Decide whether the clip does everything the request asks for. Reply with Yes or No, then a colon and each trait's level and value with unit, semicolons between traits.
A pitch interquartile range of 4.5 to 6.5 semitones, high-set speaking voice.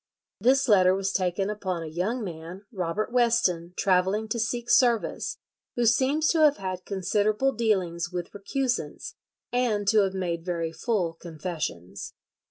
Yes: average, 4.9 semitones; high, 195 Hz